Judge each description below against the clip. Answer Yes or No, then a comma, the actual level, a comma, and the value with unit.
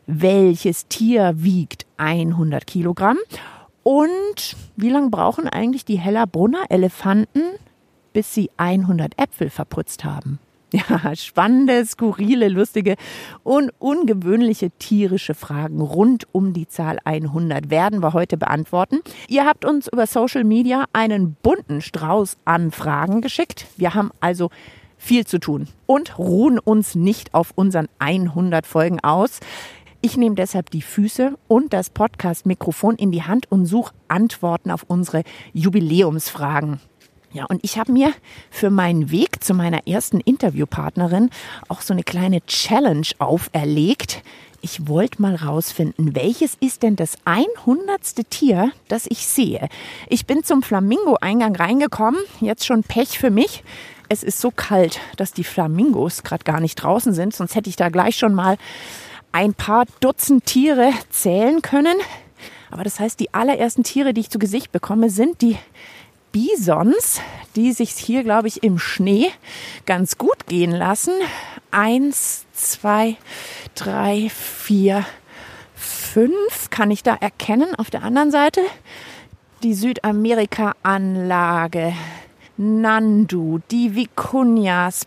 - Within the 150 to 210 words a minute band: No, average, 135 wpm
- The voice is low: No, high, 205 Hz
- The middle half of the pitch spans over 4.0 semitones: Yes, wide, 5.4 semitones